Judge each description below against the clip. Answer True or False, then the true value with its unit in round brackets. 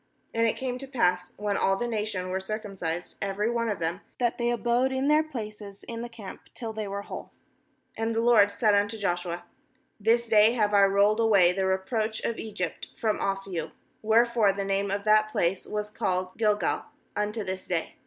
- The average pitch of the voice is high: True (210 Hz)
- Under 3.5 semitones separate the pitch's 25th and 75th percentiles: True (2.8 semitones)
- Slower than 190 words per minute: False (195 wpm)